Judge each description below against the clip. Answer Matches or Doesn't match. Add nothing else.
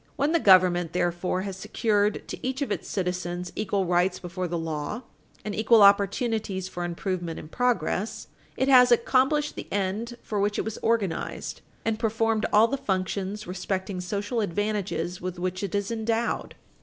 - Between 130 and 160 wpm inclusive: Doesn't match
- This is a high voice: Matches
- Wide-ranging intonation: Doesn't match